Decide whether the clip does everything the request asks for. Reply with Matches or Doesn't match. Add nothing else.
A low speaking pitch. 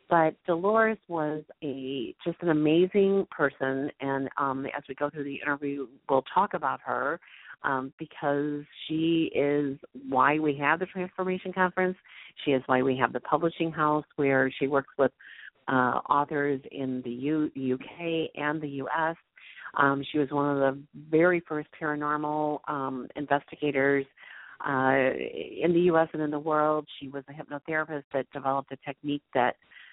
Doesn't match